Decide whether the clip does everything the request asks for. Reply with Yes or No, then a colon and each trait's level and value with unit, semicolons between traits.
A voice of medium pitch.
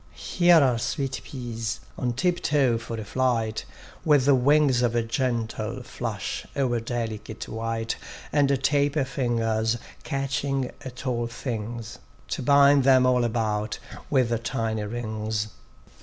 No: low, 120 Hz